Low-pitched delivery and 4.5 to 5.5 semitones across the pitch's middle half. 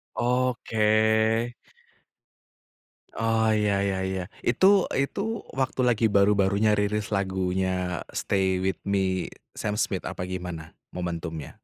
No: low, 100 Hz; narrow, 2.5 semitones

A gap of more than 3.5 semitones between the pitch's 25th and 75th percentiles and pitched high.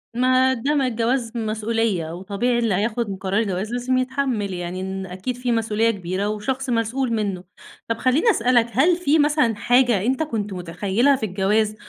Yes: average, 4.1 semitones; high, 230 Hz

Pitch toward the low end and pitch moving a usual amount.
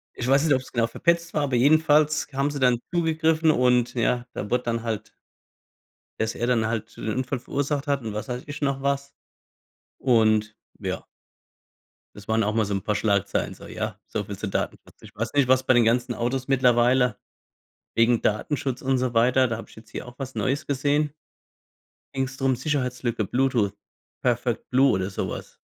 Yes: low, 125 Hz; average, 3.2 semitones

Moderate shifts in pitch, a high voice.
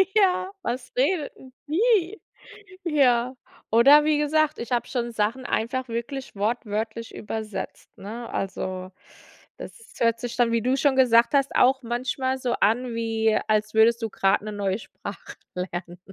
Yes: average, 3.3 semitones; high, 240 Hz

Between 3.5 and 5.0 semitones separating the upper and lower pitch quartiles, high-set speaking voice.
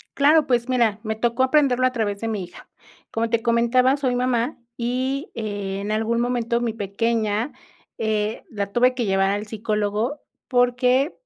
No: average, 2.8 semitones; high, 235 Hz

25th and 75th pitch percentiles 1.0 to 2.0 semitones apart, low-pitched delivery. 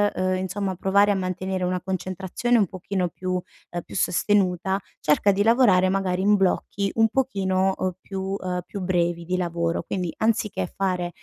No: narrow, 1.6 semitones; medium, 185 Hz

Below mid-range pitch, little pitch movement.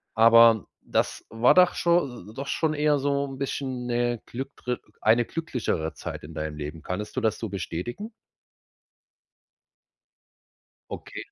No: low, 120 Hz; average, 4.3 semitones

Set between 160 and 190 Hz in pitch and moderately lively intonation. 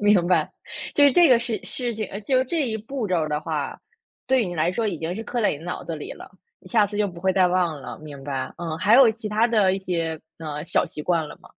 No: medium, 185 Hz; wide, 5.7 semitones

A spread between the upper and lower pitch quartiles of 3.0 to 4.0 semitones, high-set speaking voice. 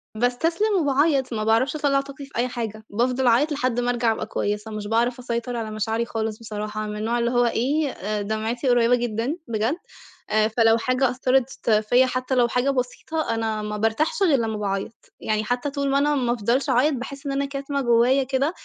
Yes: average, 3.6 semitones; high, 245 Hz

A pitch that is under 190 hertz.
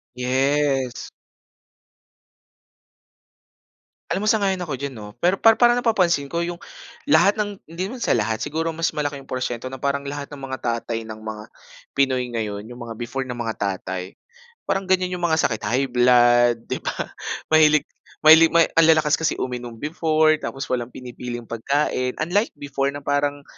Yes: medium, 140 Hz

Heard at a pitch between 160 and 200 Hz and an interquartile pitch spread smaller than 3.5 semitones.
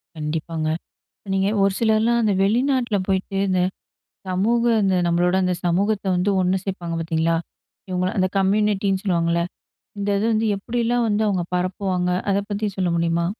Yes: high, 190 Hz; average, 2.9 semitones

